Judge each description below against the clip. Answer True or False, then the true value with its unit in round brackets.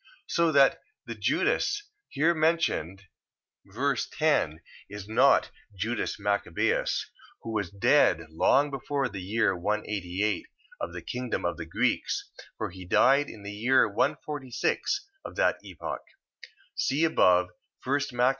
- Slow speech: True (130 wpm)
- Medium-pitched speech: False (115 Hz)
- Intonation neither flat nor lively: False (6.3 semitones)